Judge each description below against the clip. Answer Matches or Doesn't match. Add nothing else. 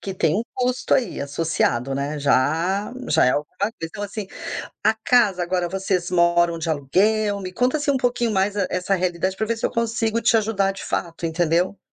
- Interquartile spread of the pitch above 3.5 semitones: Matches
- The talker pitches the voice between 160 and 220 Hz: Matches